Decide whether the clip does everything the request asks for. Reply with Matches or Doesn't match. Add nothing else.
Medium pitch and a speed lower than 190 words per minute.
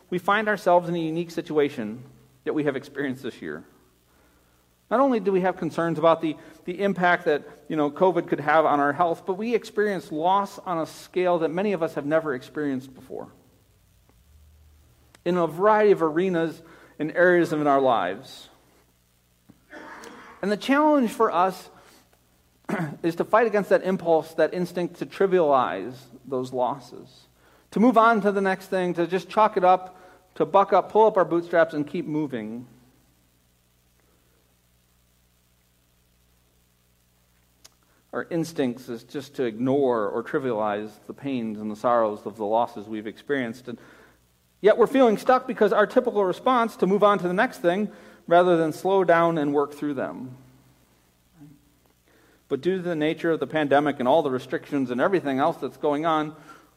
Matches